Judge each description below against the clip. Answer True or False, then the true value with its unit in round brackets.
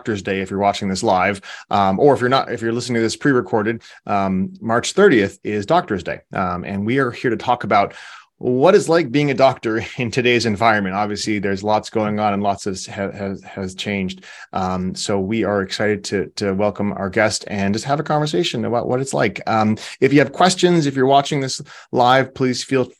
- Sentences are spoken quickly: True (220 wpm)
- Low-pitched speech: True (110 Hz)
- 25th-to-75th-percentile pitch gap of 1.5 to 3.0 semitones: False (4.4 semitones)